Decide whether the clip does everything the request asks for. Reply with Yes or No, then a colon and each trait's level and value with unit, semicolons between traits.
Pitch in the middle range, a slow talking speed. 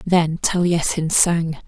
Yes: medium, 165 Hz; slow, 110 wpm